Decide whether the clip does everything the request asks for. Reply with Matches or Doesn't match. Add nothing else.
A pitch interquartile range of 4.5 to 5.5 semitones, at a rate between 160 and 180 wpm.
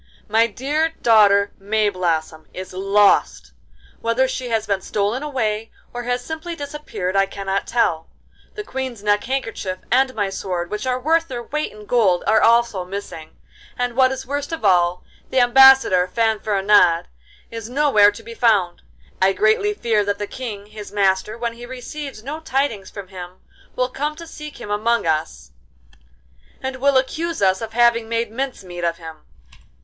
Matches